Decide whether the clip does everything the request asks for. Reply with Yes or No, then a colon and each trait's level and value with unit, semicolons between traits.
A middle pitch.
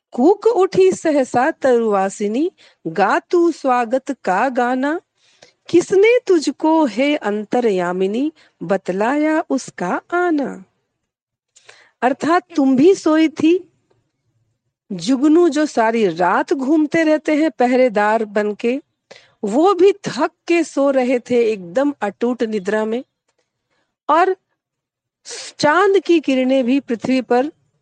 No: very high, 270 Hz